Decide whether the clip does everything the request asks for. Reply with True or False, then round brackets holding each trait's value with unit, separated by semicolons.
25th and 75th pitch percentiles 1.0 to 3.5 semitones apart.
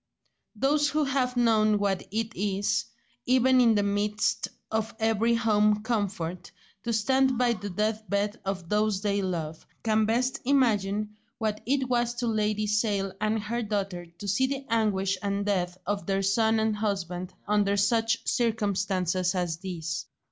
True (2.6 semitones)